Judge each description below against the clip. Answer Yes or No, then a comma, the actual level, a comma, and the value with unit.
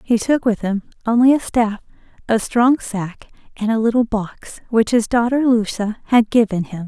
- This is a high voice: Yes, high, 225 Hz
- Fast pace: No, average, 185 wpm